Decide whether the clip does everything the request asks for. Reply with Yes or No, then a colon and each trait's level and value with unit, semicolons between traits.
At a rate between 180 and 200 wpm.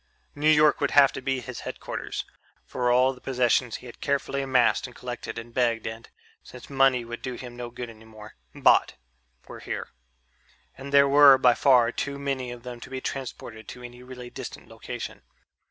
Yes: average, 190 wpm